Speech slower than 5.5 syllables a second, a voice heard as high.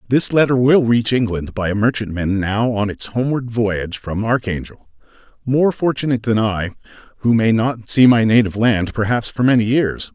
No: 5.2 syllables/s; low, 115 Hz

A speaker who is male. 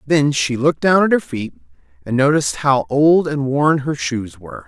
Yes: male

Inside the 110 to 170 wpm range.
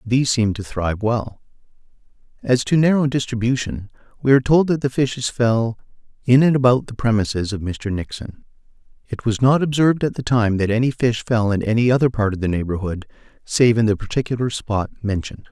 No: average, 185 wpm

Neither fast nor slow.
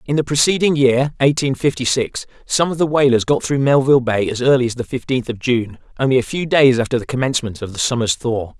No: fast, 230 wpm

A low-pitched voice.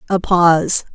No: medium, 175 Hz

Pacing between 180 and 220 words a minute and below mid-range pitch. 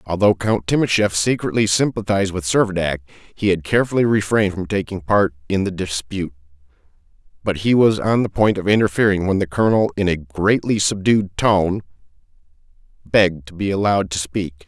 No: average, 160 wpm; very low, 95 Hz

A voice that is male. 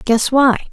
No: female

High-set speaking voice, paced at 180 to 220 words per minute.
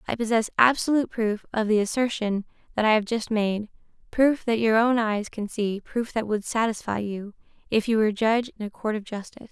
Yes: high, 220 Hz; average, 195 wpm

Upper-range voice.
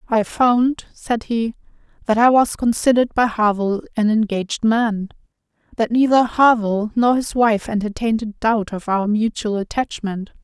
Yes: high, 225 Hz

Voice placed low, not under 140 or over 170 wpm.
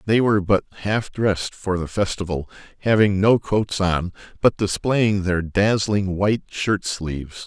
Yes: low, 100 Hz; average, 155 wpm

